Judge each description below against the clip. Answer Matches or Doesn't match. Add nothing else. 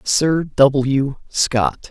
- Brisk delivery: Doesn't match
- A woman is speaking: Doesn't match